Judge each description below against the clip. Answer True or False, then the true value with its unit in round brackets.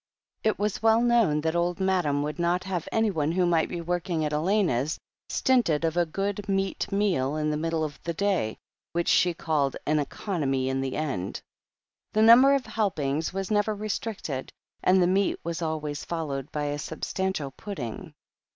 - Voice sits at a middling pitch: True (170 Hz)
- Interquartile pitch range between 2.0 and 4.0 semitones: False (4.7 semitones)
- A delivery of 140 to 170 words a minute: False (180 wpm)